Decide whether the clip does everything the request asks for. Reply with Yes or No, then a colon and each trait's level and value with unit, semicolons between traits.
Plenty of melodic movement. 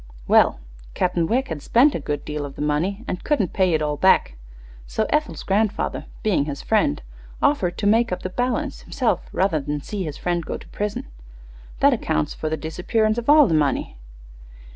Yes: wide, 6.7 semitones